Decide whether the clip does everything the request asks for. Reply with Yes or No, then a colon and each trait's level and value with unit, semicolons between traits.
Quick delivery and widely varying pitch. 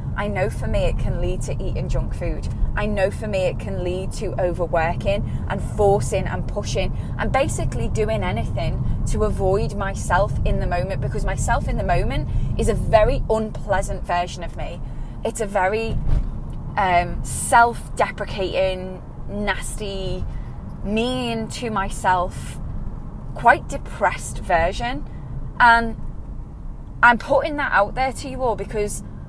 No: average, 140 wpm; wide, 9.0 semitones